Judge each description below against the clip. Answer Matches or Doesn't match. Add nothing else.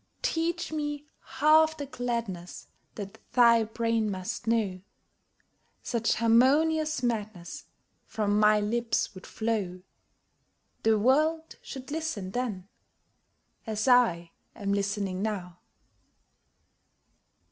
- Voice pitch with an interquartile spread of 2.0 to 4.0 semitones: Doesn't match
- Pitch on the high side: Matches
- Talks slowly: Matches